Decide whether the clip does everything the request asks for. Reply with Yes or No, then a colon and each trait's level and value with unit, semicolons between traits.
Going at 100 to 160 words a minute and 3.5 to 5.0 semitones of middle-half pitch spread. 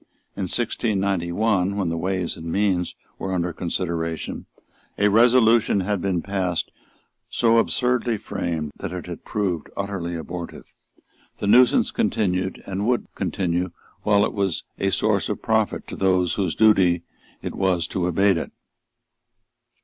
No: slow, 135 wpm; average, 3.0 semitones